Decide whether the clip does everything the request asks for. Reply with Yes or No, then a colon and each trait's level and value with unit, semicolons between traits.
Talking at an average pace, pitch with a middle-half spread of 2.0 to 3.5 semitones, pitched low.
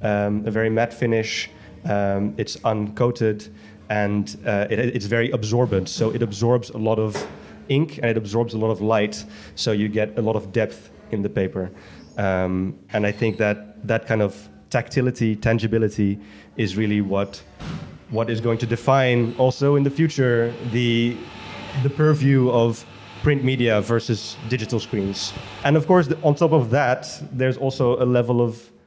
Yes: average, 170 wpm; average, 2.9 semitones; low, 115 Hz